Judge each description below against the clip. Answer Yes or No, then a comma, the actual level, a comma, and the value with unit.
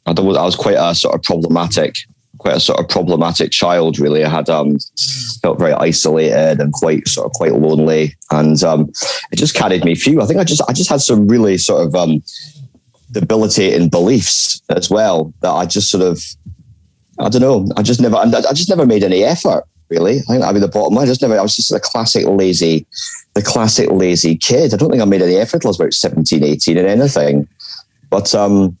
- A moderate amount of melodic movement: Yes, average, 3.9 semitones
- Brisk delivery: Yes, fast, 215 wpm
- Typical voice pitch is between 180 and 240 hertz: No, very low, 85 Hz